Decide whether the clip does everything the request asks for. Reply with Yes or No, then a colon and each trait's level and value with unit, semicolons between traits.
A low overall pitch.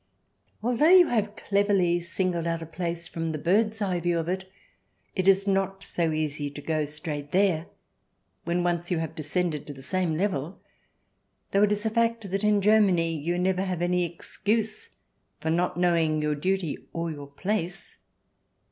No: medium, 175 Hz